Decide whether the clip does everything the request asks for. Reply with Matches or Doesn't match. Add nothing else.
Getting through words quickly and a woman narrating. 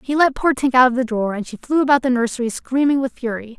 Matches